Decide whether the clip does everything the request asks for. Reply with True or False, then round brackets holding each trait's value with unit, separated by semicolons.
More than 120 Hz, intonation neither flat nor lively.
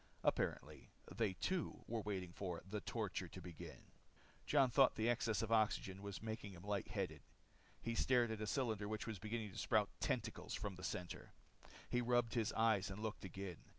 False (105 Hz; 3.1 semitones)